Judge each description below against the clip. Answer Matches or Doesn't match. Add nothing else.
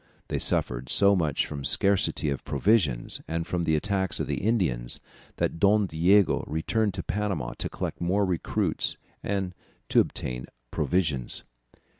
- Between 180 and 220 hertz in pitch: Doesn't match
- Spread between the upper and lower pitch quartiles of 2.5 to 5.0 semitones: Doesn't match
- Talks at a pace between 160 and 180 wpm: Doesn't match